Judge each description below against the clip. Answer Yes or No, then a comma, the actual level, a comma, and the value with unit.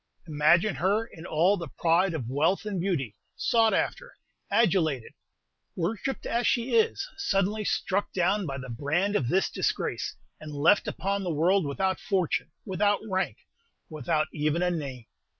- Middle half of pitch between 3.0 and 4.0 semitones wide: No, average, 4.8 semitones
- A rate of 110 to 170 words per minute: Yes, average, 150 wpm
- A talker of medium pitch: Yes, medium, 180 Hz